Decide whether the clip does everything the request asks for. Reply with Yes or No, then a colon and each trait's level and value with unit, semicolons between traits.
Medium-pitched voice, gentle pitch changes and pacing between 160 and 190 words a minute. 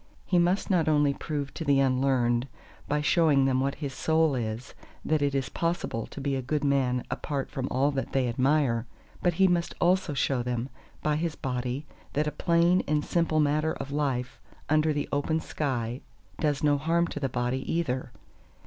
No: medium, 145 Hz; average, 3.1 semitones; average, 185 wpm